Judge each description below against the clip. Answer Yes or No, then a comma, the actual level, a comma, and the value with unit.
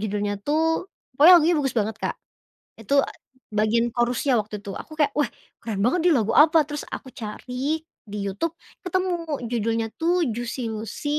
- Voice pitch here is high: Yes, high, 240 Hz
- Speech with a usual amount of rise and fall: No, wide, 5.7 semitones